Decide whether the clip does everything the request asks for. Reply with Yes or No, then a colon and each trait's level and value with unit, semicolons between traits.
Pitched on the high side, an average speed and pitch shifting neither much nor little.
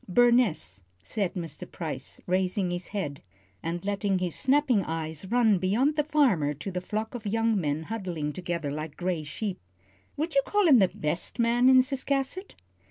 No: high, 195 Hz; average, 165 wpm; wide, 6.5 semitones